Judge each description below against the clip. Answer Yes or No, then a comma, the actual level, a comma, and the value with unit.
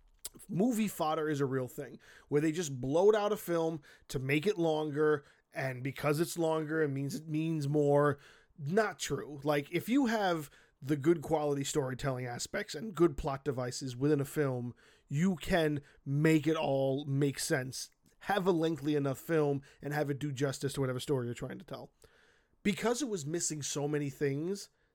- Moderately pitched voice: Yes, medium, 150 Hz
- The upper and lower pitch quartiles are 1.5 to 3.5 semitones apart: Yes, average, 2.8 semitones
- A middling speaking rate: Yes, average, 180 wpm